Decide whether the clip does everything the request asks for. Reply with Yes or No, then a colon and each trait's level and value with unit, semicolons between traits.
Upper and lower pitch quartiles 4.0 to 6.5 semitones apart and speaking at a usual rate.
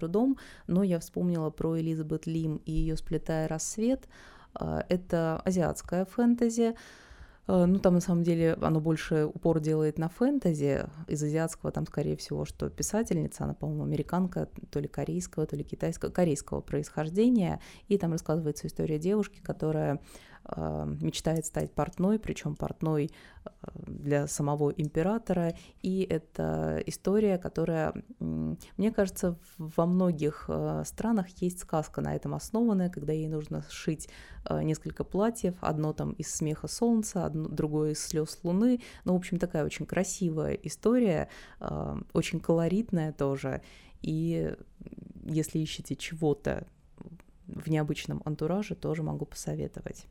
No: average, 3.5 semitones; average, 125 wpm